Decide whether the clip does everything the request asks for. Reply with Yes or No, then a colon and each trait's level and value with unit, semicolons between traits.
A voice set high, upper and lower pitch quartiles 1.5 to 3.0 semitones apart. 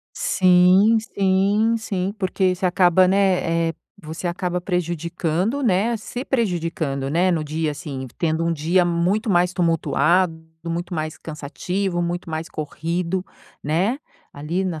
No: medium, 175 Hz; narrow, 2.6 semitones